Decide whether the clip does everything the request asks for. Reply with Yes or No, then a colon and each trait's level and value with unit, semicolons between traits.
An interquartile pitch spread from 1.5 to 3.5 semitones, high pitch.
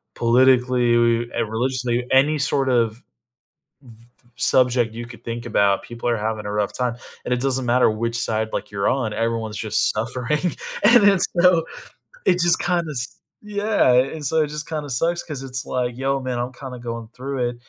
No: average, 2.8 semitones; low, 125 Hz